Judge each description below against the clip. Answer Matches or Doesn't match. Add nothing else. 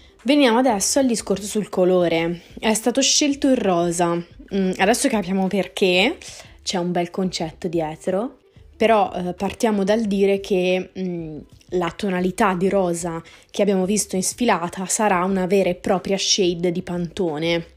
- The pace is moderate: Matches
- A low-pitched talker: Doesn't match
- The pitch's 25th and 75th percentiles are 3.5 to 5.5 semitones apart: Doesn't match